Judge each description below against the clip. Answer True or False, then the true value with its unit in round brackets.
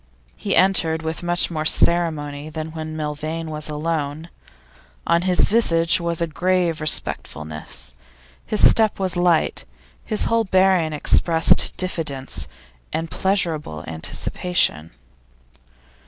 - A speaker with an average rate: False (110 wpm)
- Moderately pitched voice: True (165 Hz)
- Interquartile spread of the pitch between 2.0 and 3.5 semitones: True (2.8 semitones)